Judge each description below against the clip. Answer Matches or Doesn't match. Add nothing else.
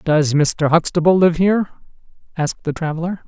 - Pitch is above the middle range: Doesn't match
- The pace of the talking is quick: Doesn't match